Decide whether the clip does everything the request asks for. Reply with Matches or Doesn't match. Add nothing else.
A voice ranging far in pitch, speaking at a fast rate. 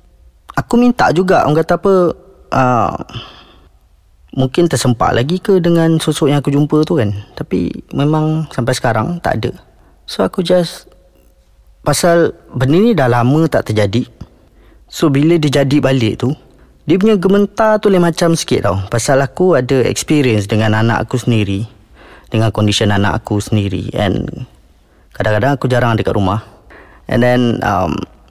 Matches